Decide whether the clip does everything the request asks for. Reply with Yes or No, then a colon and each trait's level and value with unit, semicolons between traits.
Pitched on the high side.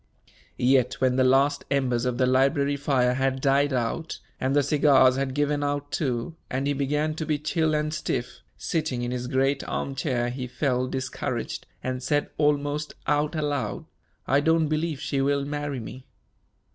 No: medium, 140 Hz